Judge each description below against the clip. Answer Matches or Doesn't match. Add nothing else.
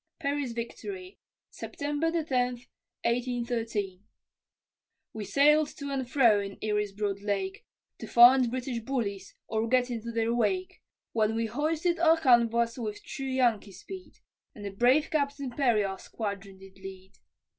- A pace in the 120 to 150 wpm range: Matches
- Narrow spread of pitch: Doesn't match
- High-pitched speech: Matches